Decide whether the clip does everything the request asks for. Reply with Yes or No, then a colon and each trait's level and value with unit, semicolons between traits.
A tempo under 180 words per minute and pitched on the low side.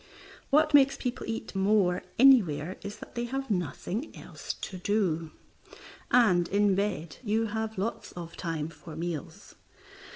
No: average, 140 wpm; high, 200 Hz